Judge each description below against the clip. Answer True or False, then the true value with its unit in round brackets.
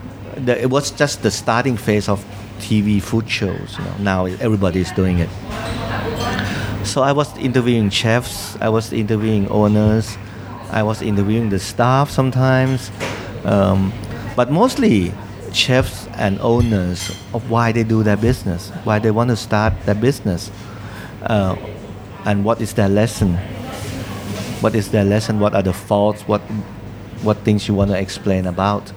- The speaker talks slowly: False (150 wpm)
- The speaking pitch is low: True (105 Hz)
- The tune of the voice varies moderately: False (2.3 semitones)